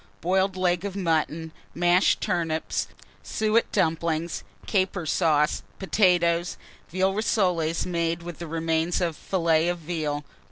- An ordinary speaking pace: No, slow, 115 wpm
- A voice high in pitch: No, medium, 170 Hz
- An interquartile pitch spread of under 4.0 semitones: Yes, narrow, 2.4 semitones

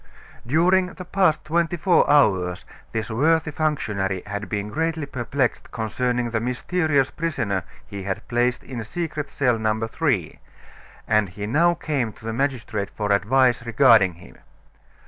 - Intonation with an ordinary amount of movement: No, wide, 6.2 semitones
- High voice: No, low, 120 Hz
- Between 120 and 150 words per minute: Yes, average, 145 wpm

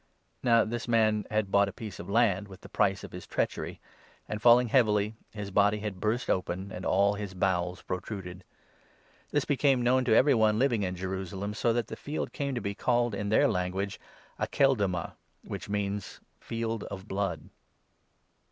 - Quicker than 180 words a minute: Yes, average, 190 wpm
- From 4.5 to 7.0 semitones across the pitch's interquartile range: No, average, 3.3 semitones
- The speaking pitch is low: Yes, low, 105 Hz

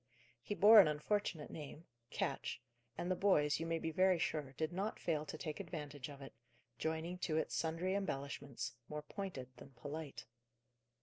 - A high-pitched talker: No, medium, 160 Hz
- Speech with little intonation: No, average, 3.6 semitones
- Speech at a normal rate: Yes, average, 170 wpm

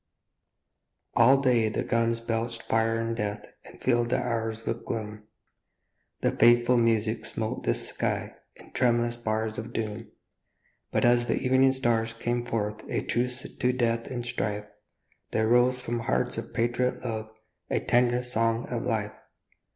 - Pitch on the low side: Yes, low, 115 Hz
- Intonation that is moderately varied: No, narrow, 1.4 semitones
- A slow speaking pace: No, average, 150 wpm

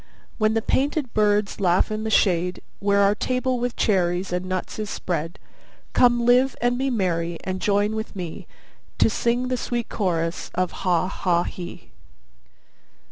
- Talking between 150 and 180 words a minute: Yes, average, 160 wpm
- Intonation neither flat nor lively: Yes, average, 4.8 semitones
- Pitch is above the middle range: Yes, high, 205 Hz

